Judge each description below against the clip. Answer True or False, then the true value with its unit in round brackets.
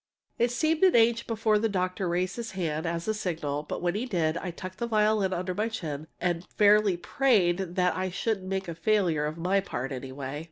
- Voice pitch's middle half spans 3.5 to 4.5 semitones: True (4.2 semitones)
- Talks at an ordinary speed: False (210 wpm)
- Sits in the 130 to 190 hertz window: True (185 Hz)